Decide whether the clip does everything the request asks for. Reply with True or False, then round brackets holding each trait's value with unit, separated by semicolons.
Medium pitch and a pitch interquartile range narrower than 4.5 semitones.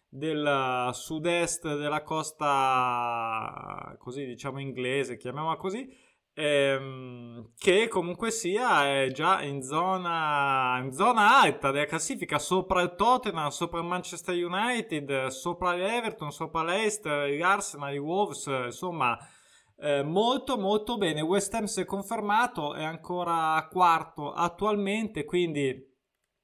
False (160 Hz; 5.0 semitones)